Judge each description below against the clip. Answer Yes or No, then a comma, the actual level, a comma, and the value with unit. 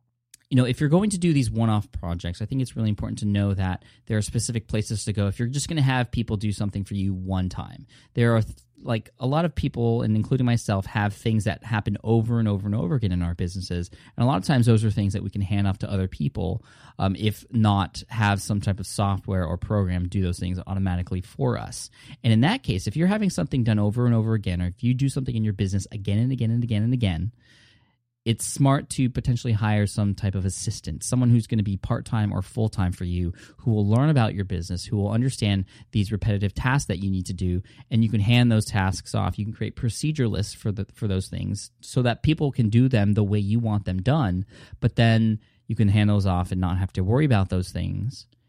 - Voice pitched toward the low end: Yes, low, 110 Hz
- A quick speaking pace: Yes, fast, 250 wpm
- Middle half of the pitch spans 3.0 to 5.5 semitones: Yes, average, 3.4 semitones